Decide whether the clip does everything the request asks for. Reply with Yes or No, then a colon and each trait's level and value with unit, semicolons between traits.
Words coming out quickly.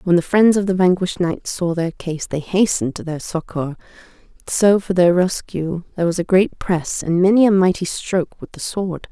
Yes: fast, 210 wpm